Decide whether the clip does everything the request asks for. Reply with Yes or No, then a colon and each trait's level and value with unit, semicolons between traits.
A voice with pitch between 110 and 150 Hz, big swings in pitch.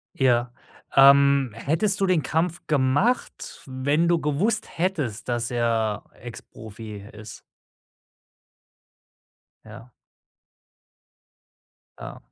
Yes: low, 135 Hz; wide, 5.8 semitones